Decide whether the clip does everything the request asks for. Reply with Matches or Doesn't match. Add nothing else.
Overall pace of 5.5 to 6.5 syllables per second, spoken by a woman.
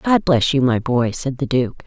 Doesn't match